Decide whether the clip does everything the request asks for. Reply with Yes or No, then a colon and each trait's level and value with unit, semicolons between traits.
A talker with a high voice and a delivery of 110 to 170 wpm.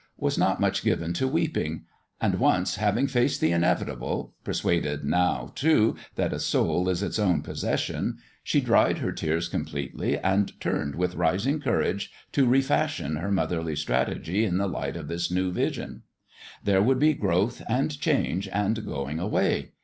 No: very low, 95 Hz; average, 165 wpm